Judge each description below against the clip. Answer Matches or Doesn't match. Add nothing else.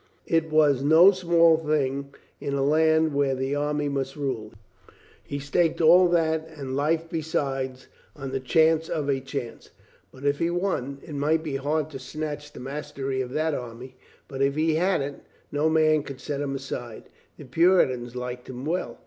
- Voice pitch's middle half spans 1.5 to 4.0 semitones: Matches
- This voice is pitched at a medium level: Matches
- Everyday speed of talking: Matches